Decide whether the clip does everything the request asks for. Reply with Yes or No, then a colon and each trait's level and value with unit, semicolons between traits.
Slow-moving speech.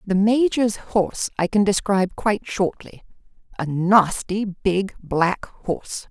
Yes: slow, 120 wpm